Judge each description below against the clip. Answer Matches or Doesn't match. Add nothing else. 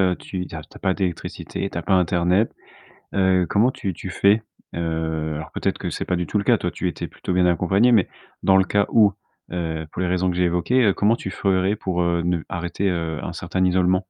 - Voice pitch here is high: Doesn't match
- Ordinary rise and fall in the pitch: Doesn't match